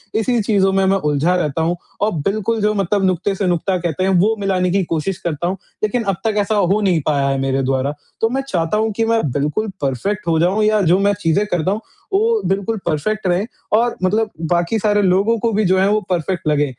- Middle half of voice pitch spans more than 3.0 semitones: Yes, average, 4.0 semitones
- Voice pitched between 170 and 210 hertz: Yes, high, 190 Hz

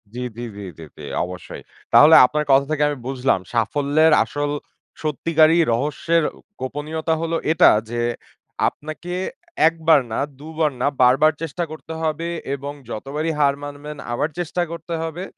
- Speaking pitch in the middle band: Yes, medium, 150 Hz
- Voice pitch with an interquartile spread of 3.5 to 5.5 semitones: No, average, 2.9 semitones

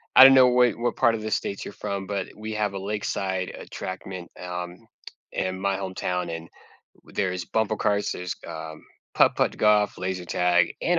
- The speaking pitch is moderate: No, very low, 95 Hz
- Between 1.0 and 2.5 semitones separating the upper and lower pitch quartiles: No, average, 2.9 semitones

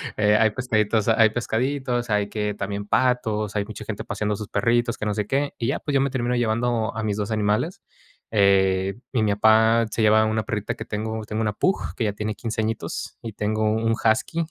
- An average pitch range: No, narrow, 1.9 semitones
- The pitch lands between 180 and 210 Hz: No, low, 110 Hz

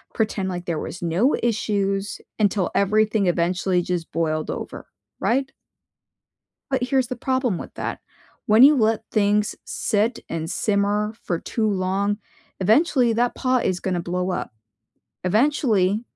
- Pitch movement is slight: No, average, 4.0 semitones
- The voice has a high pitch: Yes, high, 205 Hz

